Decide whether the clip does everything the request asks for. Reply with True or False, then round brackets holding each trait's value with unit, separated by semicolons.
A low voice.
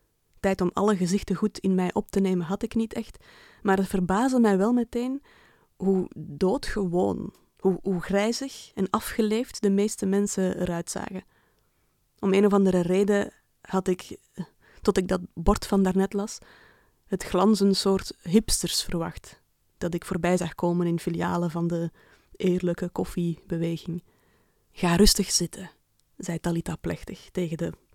False (190 Hz)